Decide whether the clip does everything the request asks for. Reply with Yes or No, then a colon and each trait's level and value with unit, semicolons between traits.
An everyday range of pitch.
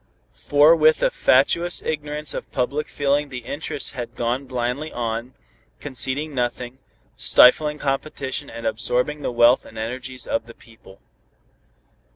Yes: average, 3.5 semitones